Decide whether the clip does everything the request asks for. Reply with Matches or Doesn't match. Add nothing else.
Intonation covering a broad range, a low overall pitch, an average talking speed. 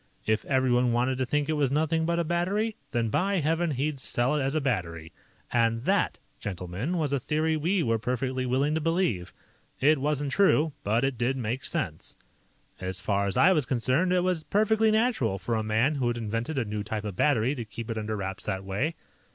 Doesn't match